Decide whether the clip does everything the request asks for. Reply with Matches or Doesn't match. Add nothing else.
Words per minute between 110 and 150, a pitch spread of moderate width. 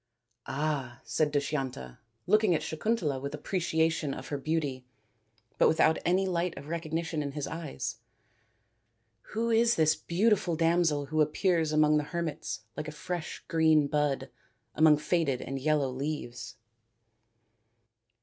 Matches